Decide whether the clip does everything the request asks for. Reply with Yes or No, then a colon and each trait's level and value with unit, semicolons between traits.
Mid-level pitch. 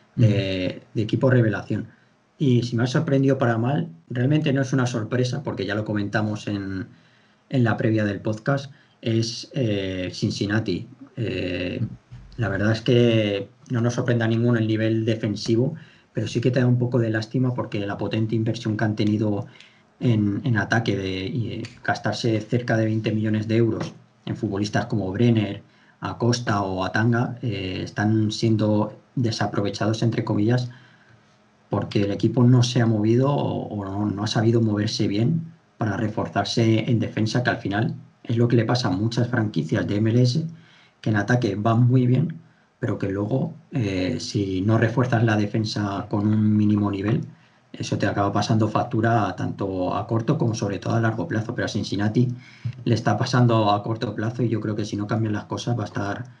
No: low, 115 Hz